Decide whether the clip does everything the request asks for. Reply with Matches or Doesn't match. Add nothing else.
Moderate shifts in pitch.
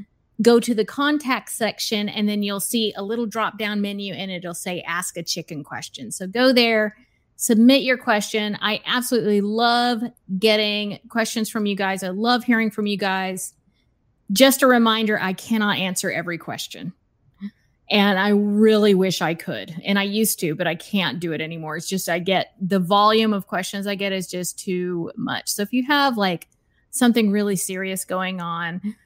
Matches